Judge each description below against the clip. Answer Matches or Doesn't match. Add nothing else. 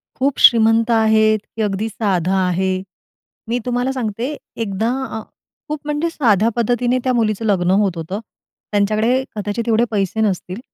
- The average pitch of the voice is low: Doesn't match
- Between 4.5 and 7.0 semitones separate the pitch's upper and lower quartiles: Doesn't match